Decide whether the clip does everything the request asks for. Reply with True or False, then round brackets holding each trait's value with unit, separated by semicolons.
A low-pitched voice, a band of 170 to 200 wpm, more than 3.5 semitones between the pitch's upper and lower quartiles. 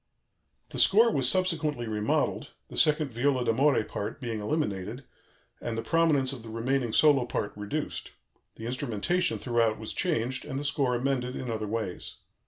False (125 Hz; 160 wpm; 4.5 semitones)